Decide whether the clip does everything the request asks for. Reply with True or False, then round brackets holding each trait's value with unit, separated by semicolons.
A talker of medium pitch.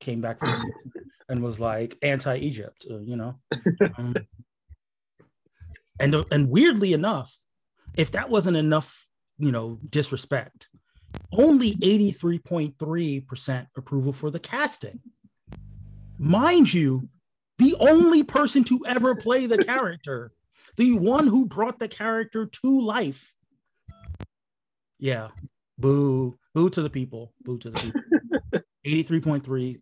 True (150 Hz)